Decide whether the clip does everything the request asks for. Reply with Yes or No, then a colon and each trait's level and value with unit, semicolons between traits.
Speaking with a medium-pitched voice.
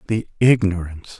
No: low, 100 Hz